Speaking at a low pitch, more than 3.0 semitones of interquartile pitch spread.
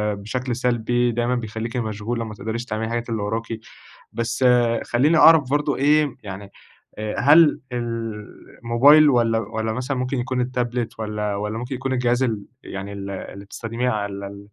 No: low, 115 Hz; average, 2.7 semitones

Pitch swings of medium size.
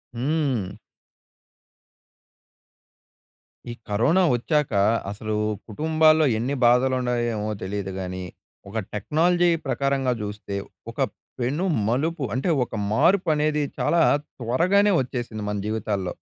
No: wide, 6.3 semitones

